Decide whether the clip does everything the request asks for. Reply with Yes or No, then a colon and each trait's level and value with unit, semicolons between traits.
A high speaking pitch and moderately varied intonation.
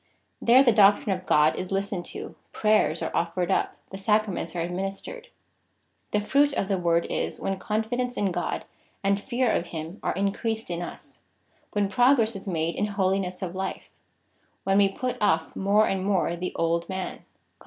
Yes: high, 195 Hz; average, 3.1 semitones